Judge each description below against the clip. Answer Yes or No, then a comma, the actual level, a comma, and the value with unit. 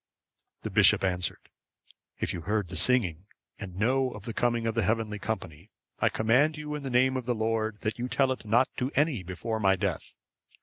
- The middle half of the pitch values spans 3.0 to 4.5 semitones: Yes, average, 3.6 semitones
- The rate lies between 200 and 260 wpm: Yes, fast, 205 wpm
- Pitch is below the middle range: Yes, low, 115 Hz